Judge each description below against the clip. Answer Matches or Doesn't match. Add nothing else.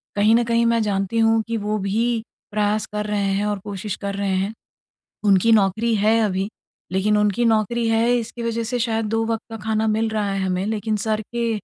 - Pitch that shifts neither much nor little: Doesn't match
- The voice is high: Matches